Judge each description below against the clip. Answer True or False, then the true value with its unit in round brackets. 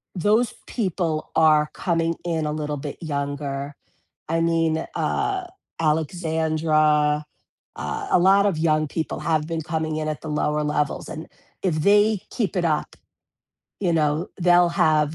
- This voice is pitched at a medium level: True (160 Hz)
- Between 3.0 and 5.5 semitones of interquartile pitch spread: False (2.4 semitones)